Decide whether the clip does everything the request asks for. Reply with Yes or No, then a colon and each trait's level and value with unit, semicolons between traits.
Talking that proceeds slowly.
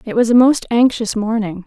No: fast, 215 wpm